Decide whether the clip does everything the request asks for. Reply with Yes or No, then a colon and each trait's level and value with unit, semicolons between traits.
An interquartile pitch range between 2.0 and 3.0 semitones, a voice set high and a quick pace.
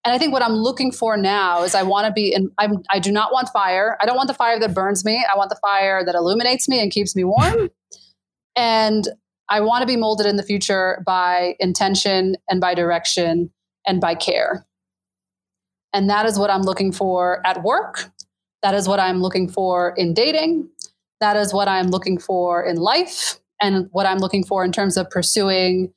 Yes: average, 2.7 semitones; high, 195 Hz; fast, 210 wpm